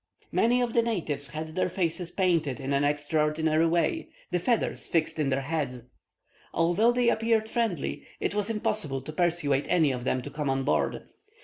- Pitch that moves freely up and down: Yes, wide, 6.3 semitones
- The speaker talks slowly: No, average, 180 wpm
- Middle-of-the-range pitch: Yes, medium, 165 Hz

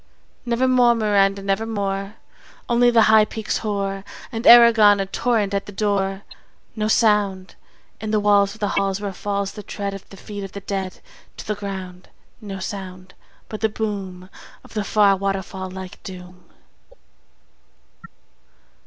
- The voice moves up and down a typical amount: No, narrow, 1.8 semitones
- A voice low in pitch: No, high, 200 Hz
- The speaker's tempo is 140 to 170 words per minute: Yes, average, 155 wpm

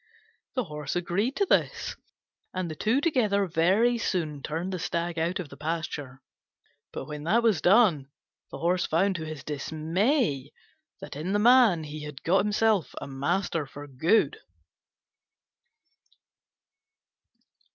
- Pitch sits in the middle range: Yes, medium, 170 Hz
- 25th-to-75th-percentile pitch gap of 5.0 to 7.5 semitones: Yes, average, 5.3 semitones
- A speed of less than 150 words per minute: Yes, slow, 135 wpm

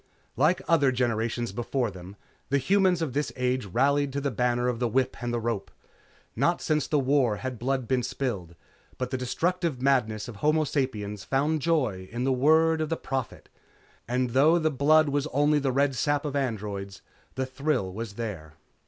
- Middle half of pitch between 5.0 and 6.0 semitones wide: No, average, 3.7 semitones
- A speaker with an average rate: Yes, average, 185 wpm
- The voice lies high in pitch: No, low, 130 Hz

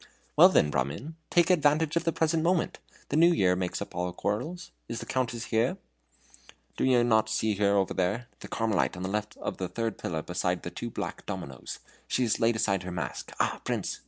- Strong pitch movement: Yes, wide, 7.9 semitones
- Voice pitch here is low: Yes, low, 110 Hz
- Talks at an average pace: No, fast, 210 wpm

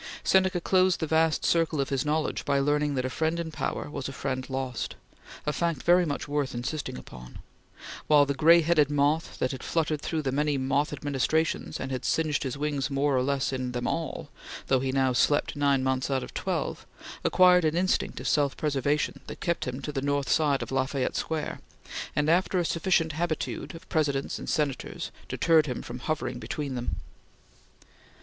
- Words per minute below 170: No, average, 195 wpm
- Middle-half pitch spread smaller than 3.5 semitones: Yes, average, 3.0 semitones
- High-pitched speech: No, medium, 145 Hz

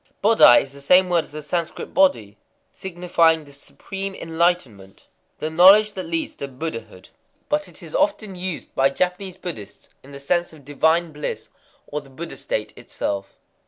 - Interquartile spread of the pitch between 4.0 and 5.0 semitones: Yes, average, 4.5 semitones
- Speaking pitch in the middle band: Yes, medium, 165 Hz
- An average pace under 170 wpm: Yes, average, 160 wpm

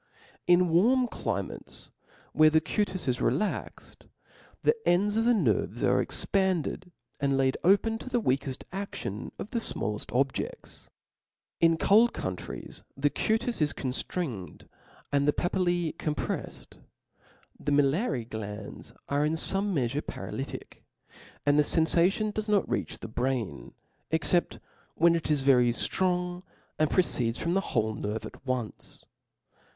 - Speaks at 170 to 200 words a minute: No, average, 140 wpm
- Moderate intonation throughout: No, wide, 6.4 semitones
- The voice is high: No, medium, 160 Hz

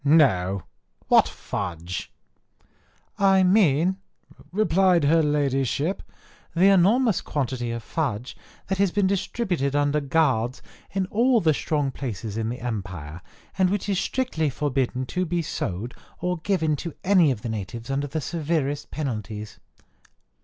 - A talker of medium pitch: Yes, medium, 145 Hz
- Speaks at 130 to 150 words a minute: Yes, slow, 135 wpm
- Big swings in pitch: Yes, wide, 7.0 semitones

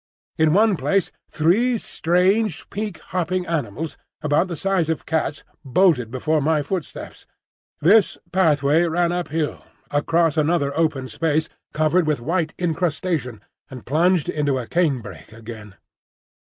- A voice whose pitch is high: No, medium, 160 Hz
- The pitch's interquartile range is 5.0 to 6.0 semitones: No, average, 3.6 semitones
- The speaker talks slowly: Yes, slow, 130 wpm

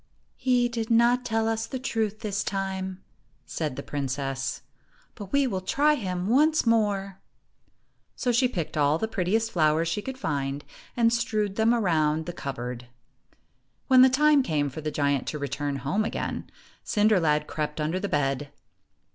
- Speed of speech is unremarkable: Yes, average, 165 wpm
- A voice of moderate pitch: No, high, 195 Hz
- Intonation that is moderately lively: No, wide, 7.3 semitones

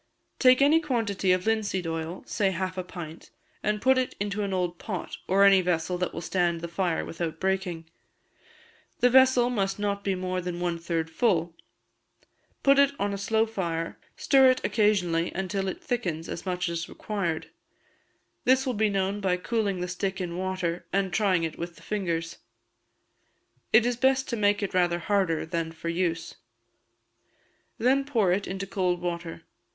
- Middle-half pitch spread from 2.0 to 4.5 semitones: Yes, average, 3.6 semitones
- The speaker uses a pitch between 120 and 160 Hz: No, high, 190 Hz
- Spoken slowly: No, average, 170 wpm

